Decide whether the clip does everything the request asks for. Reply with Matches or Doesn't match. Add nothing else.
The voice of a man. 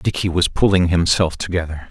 Matches